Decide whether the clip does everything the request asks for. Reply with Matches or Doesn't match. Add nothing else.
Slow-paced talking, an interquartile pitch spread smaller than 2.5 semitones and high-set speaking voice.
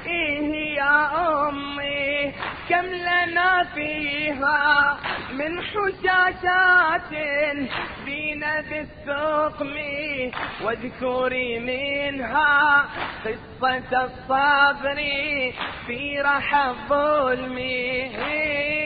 Matches